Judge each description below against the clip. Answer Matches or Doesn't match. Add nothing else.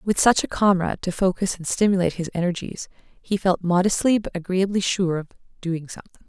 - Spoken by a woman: Matches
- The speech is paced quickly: Doesn't match